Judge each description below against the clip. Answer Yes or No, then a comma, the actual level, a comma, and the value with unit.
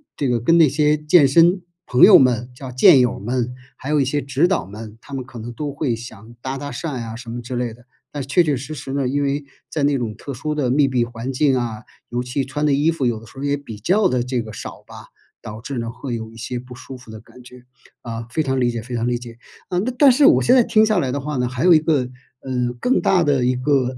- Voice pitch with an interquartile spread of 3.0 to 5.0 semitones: Yes, average, 3.3 semitones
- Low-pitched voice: Yes, low, 130 Hz